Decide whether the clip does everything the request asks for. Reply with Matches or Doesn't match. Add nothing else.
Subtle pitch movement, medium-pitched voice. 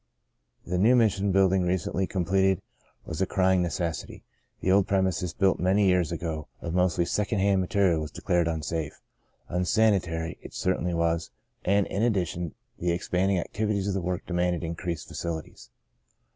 Doesn't match